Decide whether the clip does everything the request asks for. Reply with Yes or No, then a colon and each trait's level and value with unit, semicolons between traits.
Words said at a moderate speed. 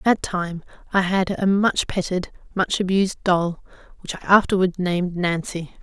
Yes: average, 165 wpm